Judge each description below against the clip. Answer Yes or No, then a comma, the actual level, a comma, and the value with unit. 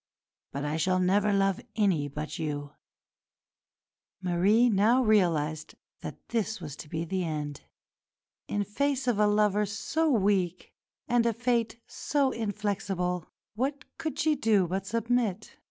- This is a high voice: Yes, high, 205 Hz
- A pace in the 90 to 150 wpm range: Yes, average, 140 wpm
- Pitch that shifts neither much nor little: Yes, average, 4.5 semitones